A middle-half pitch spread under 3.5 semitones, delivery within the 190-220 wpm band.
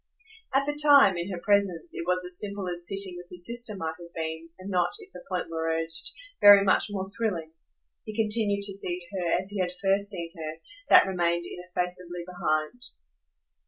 Yes: average, 2.8 semitones; average, 195 wpm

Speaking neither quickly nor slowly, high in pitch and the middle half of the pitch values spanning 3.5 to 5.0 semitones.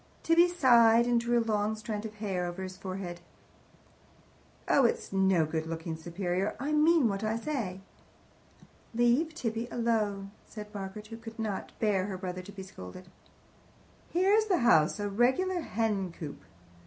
Yes: average, 155 wpm; high, 210 Hz; average, 4.1 semitones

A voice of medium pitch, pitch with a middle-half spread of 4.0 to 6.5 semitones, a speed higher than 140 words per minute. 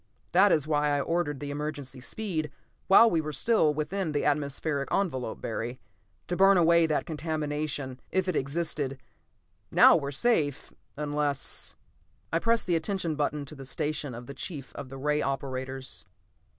No: medium, 150 Hz; average, 3.2 semitones; average, 165 wpm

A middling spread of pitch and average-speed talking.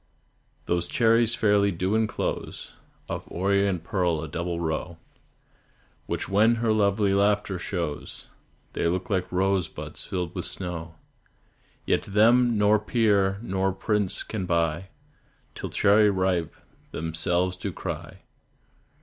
No: average, 3.1 semitones; slow, 125 wpm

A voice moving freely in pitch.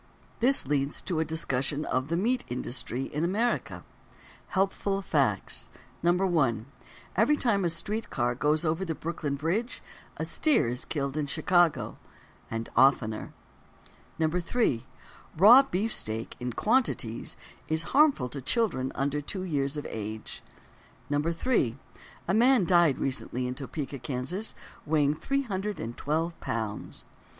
Yes: wide, 6.5 semitones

